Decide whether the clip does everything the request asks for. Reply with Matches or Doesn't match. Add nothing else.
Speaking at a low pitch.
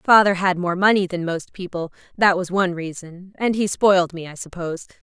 Doesn't match